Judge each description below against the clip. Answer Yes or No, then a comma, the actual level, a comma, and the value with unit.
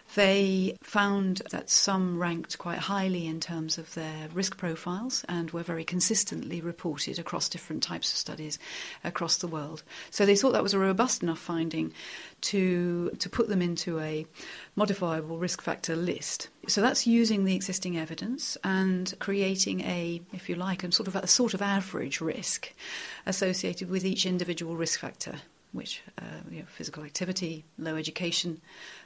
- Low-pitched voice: No, medium, 180 Hz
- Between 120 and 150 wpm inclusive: No, average, 165 wpm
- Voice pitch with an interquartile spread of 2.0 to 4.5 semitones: Yes, average, 2.9 semitones